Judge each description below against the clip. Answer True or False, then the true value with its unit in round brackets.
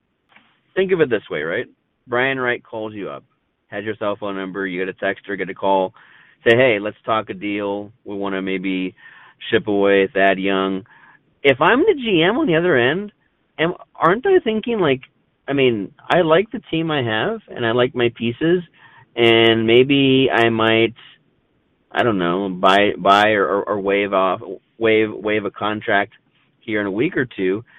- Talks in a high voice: False (110 Hz)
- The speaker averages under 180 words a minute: False (190 wpm)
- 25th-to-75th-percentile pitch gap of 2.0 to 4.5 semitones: False (5.1 semitones)